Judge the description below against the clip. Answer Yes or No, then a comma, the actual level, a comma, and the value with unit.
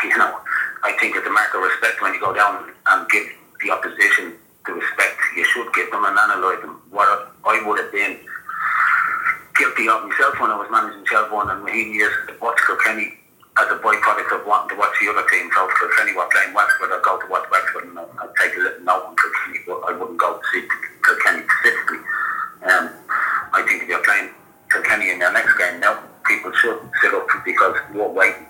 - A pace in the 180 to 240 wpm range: Yes, fast, 205 wpm